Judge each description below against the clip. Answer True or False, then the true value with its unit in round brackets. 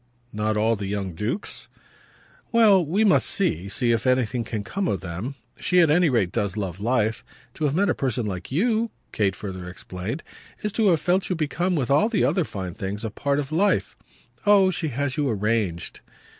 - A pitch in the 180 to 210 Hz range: False (125 Hz)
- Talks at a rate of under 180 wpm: False (200 wpm)